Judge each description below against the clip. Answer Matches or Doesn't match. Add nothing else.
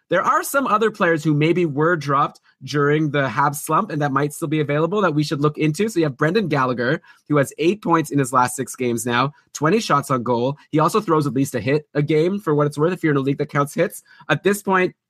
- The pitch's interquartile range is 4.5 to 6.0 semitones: Doesn't match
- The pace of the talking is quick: Matches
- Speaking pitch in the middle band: Matches